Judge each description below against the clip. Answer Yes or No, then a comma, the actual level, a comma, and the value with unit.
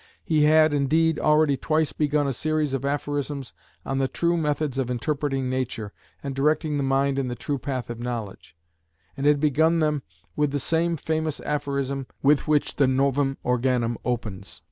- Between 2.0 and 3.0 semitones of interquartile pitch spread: Yes, narrow, 2.5 semitones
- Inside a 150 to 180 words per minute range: Yes, average, 170 wpm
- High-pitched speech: No, medium, 140 Hz